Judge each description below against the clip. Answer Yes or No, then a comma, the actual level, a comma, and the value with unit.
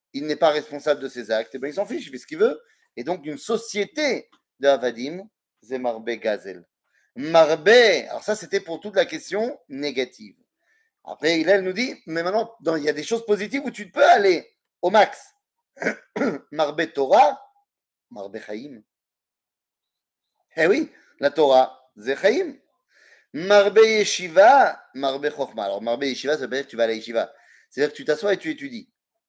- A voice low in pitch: No, medium, 185 Hz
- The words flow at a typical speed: Yes, average, 170 wpm